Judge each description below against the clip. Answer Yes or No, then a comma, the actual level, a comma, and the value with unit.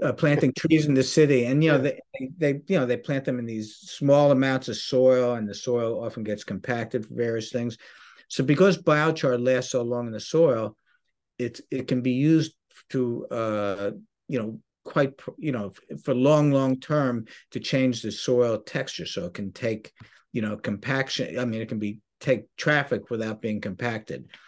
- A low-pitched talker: Yes, low, 125 Hz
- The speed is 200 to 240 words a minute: No, average, 190 wpm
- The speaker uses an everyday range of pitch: Yes, average, 3.8 semitones